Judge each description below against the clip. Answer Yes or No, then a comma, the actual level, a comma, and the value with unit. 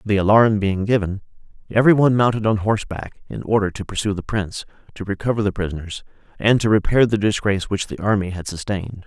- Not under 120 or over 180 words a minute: No, average, 190 wpm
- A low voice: Yes, low, 100 Hz